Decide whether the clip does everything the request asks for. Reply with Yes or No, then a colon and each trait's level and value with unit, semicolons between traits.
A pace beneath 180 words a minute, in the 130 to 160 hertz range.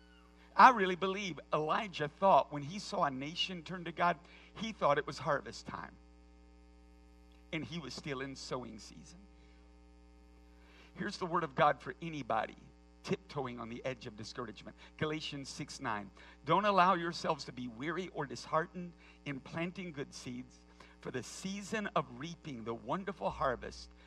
Yes: average, 155 wpm; medium, 140 Hz